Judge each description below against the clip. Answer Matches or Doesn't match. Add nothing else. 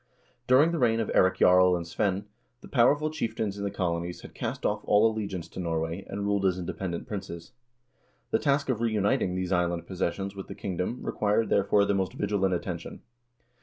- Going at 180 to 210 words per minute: Matches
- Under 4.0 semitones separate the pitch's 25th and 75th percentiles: Matches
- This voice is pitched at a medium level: Doesn't match